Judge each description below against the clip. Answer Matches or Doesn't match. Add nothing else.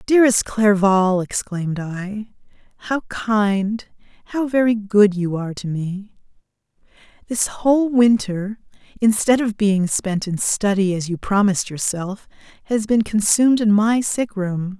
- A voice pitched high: Matches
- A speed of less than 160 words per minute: Matches